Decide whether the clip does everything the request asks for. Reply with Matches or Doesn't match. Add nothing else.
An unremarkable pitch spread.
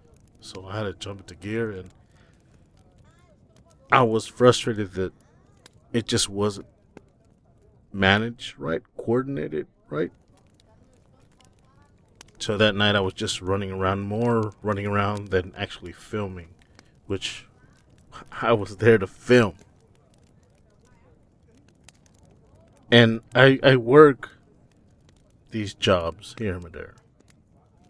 Matches